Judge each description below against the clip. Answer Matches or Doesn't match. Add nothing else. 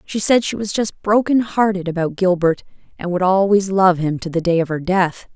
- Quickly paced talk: Matches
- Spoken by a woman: Matches